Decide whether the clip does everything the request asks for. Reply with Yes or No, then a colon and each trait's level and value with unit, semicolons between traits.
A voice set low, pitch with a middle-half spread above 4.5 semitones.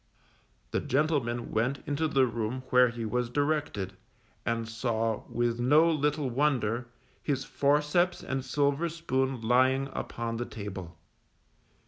No: low, 130 Hz; average, 3.7 semitones